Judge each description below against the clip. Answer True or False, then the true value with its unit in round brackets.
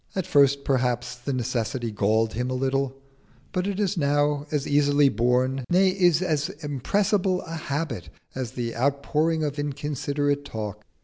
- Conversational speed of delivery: True (150 wpm)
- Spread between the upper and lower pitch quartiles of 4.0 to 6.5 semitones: False (3.5 semitones)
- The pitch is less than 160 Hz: True (140 Hz)